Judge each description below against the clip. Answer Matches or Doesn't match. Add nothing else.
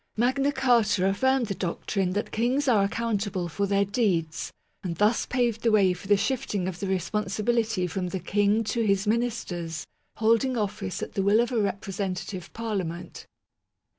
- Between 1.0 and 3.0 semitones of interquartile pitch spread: Doesn't match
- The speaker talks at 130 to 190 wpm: Matches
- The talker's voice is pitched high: Matches